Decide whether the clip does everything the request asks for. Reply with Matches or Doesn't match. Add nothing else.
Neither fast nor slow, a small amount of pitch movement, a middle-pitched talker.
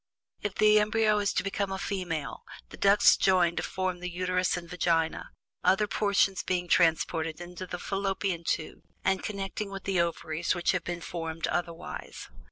Matches